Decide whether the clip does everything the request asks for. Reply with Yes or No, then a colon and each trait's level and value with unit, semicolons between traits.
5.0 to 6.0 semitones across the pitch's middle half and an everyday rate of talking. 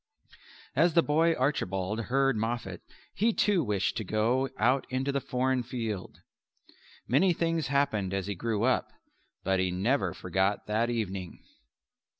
Yes: wide, 5.4 semitones; average, 145 wpm